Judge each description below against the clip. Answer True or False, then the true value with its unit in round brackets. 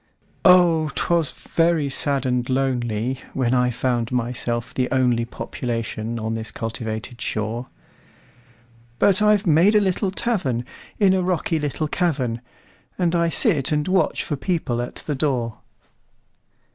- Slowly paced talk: True (120 wpm)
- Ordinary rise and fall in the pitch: False (6.0 semitones)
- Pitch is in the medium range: False (130 Hz)